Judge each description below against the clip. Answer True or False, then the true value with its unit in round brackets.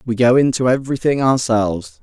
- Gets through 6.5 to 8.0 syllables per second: False (5.9 syllables/s)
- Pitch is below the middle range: True (125 Hz)